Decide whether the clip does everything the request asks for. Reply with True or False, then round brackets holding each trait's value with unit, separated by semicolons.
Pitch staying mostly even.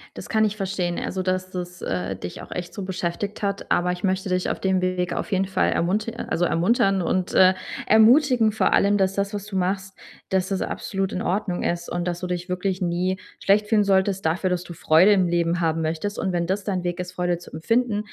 True (2.1 semitones)